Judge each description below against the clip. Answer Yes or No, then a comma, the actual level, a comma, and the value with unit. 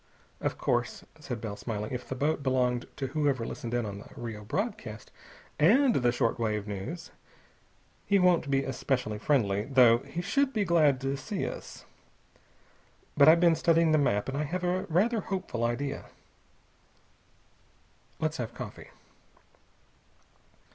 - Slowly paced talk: No, average, 145 wpm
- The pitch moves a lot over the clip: Yes, wide, 6.0 semitones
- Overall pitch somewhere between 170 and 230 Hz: No, low, 135 Hz